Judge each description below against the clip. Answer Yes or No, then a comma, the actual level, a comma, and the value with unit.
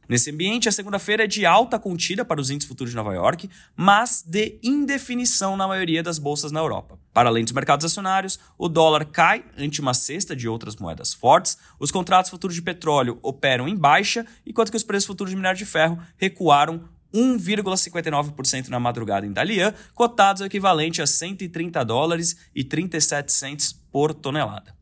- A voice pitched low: No, medium, 170 Hz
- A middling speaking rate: Yes, average, 175 wpm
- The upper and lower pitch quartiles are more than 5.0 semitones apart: Yes, wide, 5.5 semitones